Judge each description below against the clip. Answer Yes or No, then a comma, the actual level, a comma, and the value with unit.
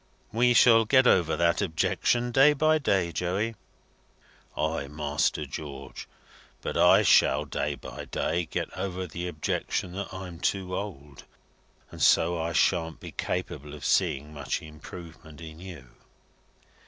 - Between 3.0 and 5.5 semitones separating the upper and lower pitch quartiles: Yes, average, 4.1 semitones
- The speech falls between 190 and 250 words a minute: No, average, 140 wpm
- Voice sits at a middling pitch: No, very low, 85 Hz